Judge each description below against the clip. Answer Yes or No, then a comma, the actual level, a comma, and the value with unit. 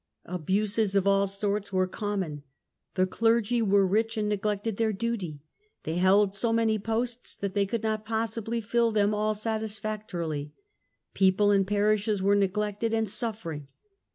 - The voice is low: No, high, 210 Hz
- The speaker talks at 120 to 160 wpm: Yes, average, 150 wpm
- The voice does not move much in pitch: Yes, narrow, 2.2 semitones